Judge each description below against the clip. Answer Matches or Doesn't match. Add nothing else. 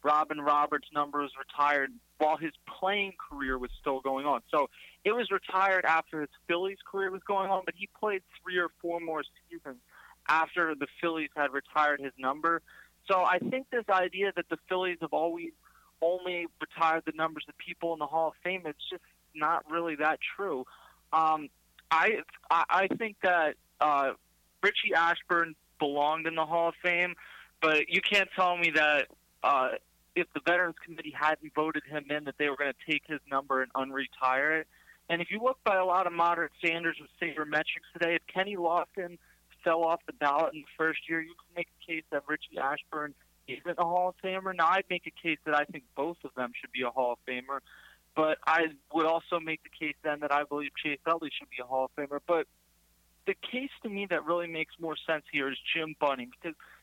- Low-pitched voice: Doesn't match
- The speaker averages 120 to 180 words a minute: Doesn't match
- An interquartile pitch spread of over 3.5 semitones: Doesn't match